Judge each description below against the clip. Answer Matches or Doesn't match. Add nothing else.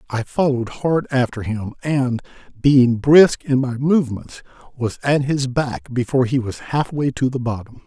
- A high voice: Doesn't match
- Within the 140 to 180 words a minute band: Matches